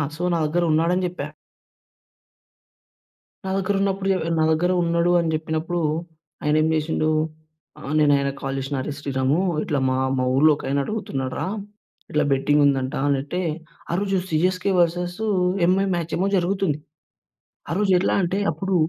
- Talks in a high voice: No, medium, 160 Hz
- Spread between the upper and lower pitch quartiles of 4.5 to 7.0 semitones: No, average, 3.9 semitones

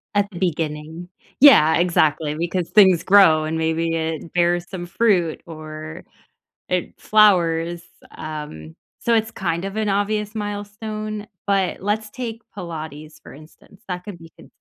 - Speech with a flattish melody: No, average, 4.3 semitones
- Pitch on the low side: No, medium, 175 Hz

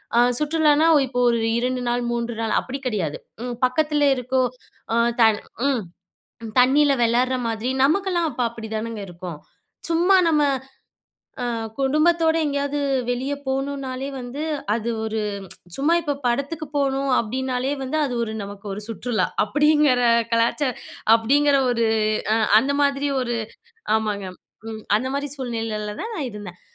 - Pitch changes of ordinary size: Yes, average, 4.0 semitones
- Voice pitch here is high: Yes, very high, 255 Hz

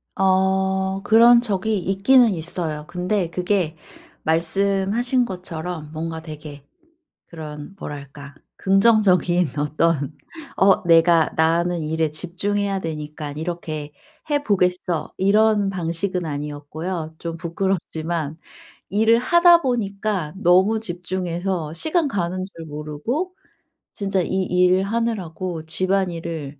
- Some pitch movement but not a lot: Yes, average, 3.6 semitones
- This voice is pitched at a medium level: Yes, medium, 180 Hz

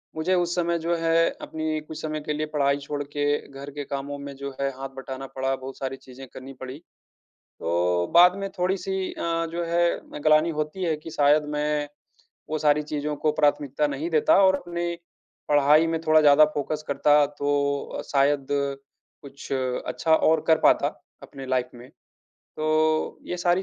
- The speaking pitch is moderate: Yes, medium, 150 Hz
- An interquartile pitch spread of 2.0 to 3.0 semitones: Yes, narrow, 2.6 semitones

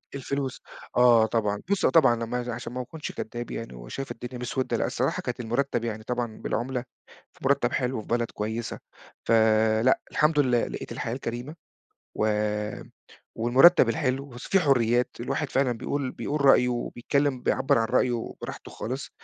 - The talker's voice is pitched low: Yes, low, 125 Hz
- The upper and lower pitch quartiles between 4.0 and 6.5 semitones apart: No, average, 2.7 semitones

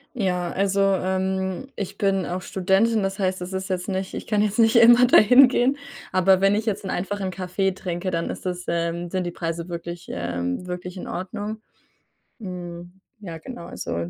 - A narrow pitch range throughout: Yes, narrow, 2.2 semitones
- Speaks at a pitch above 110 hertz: Yes, high, 190 Hz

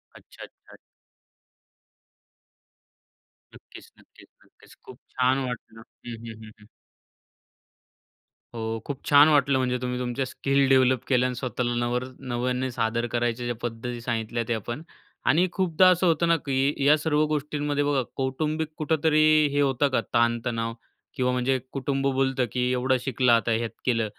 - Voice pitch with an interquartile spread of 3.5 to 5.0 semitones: No, average, 3.0 semitones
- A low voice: Yes, low, 130 Hz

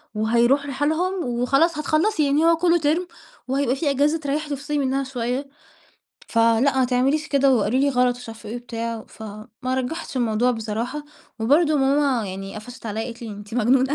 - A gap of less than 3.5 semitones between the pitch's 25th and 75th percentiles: No, average, 3.8 semitones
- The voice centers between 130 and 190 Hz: No, very high, 260 Hz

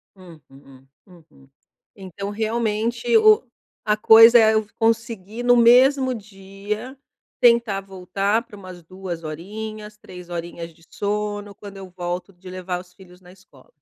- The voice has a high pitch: Yes, high, 200 Hz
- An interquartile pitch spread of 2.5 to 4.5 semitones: Yes, average, 3.6 semitones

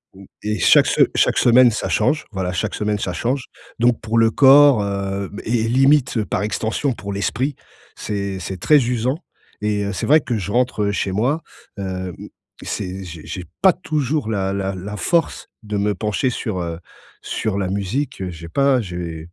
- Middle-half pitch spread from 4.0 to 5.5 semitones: Yes, average, 4.7 semitones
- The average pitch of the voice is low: Yes, low, 105 Hz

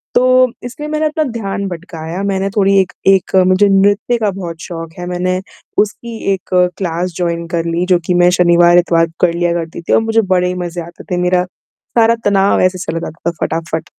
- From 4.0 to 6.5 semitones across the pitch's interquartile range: No, average, 2.7 semitones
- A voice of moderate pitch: Yes, medium, 180 Hz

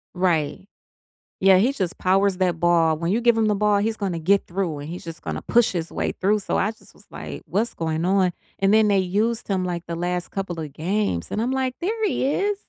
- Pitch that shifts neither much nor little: Yes, average, 3.8 semitones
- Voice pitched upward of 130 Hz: Yes, high, 190 Hz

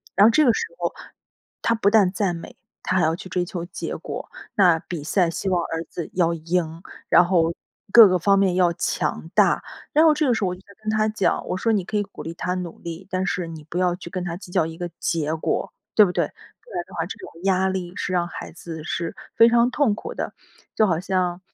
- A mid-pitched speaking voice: Yes, medium, 180 Hz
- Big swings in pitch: No, average, 3.0 semitones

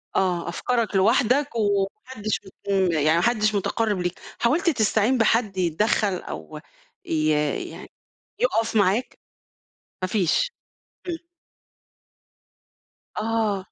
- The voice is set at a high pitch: Yes, high, 210 Hz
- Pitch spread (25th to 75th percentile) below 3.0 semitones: No, average, 3.8 semitones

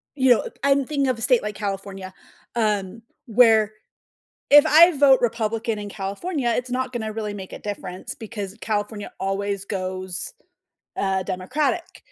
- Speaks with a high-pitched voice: Yes, high, 215 Hz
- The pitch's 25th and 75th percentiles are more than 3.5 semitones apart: Yes, average, 4.3 semitones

